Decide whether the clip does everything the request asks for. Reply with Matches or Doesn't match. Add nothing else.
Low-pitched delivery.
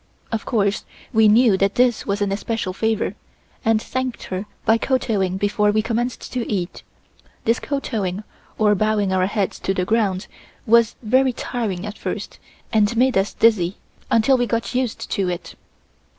Doesn't match